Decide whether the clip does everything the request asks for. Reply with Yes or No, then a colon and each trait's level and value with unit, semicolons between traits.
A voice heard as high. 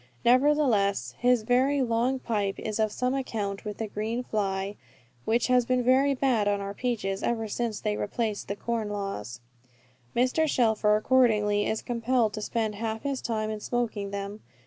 Yes: high, 220 Hz